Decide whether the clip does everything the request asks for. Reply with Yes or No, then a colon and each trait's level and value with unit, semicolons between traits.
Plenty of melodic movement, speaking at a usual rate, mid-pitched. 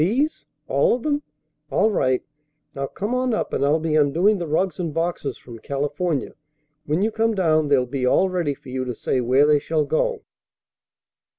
Yes: wide, 6.5 semitones; average, 190 wpm; medium, 155 Hz